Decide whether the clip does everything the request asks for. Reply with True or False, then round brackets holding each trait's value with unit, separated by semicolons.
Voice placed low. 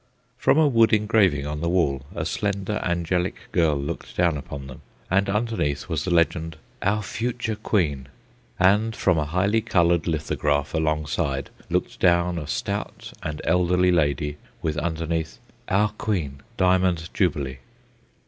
True (85 Hz)